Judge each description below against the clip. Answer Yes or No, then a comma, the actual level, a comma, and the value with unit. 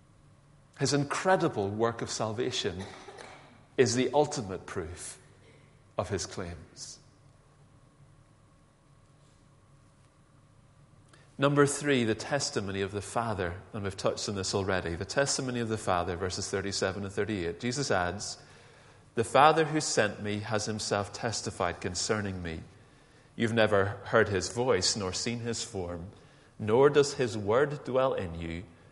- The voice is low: Yes, low, 115 Hz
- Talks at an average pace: No, slow, 130 wpm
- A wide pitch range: Yes, wide, 5.7 semitones